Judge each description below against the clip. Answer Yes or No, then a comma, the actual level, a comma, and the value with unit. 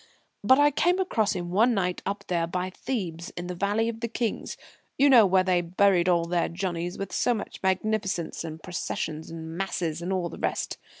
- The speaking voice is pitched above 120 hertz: Yes, medium, 185 Hz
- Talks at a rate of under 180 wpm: No, average, 200 wpm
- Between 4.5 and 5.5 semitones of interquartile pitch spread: No, average, 3.9 semitones